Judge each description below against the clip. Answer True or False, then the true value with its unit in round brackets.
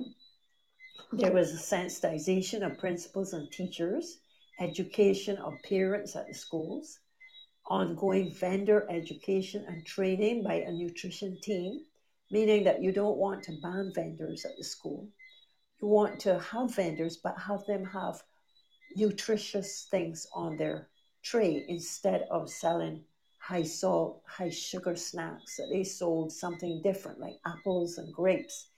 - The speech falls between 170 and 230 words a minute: False (135 wpm)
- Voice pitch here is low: False (190 Hz)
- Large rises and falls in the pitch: False (3.1 semitones)